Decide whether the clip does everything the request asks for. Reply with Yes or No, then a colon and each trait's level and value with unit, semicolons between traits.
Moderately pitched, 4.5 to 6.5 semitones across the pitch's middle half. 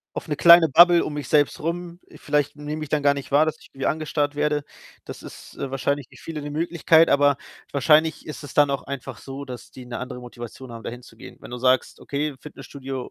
No: medium, 145 Hz; narrow, 2.5 semitones